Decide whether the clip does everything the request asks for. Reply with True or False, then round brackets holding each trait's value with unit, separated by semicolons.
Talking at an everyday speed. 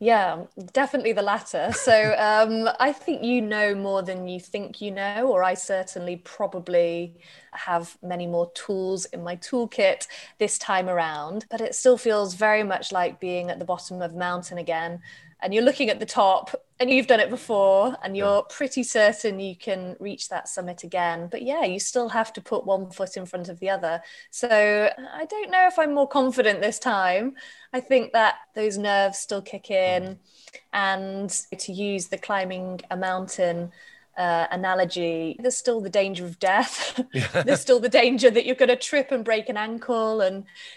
True (185 wpm)